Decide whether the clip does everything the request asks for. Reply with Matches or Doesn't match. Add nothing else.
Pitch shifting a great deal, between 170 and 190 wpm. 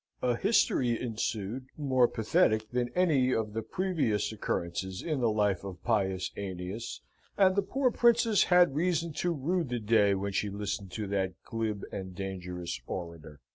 Doesn't match